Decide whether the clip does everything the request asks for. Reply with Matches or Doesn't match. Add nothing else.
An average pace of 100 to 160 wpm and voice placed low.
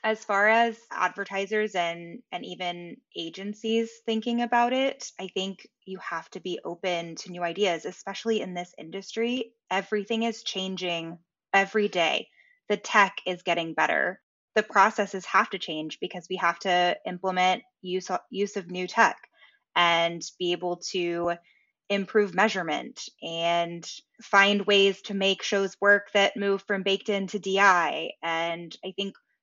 Doesn't match